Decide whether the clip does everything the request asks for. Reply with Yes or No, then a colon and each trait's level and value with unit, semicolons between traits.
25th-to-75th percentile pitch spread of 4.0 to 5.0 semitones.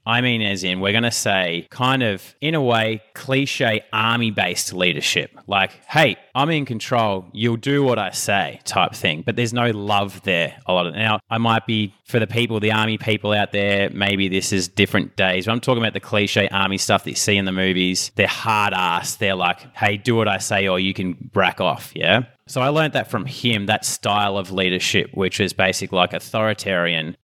No: average, 3.4 semitones